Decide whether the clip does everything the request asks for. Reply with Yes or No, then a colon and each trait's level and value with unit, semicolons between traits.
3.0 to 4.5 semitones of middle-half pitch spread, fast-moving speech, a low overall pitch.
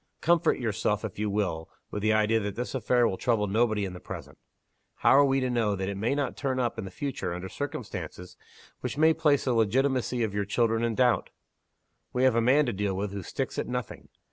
Yes: average, 4.1 semitones; fast, 220 wpm; low, 115 Hz